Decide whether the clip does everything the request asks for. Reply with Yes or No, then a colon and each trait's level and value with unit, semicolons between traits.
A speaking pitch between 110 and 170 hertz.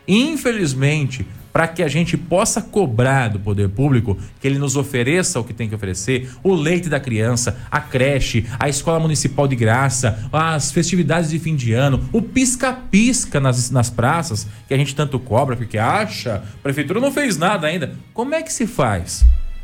Yes: medium, 140 Hz